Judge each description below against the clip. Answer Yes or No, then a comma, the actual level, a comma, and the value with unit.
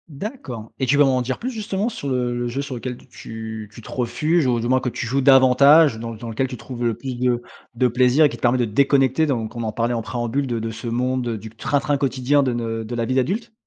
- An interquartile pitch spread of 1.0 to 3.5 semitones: Yes, average, 2.9 semitones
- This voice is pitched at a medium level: No, low, 125 Hz